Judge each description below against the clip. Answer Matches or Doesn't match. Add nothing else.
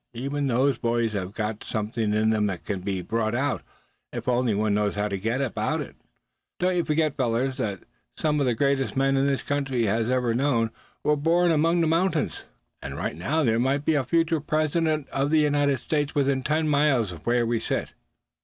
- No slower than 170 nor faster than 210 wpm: Matches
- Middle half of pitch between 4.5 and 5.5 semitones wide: Matches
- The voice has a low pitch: Matches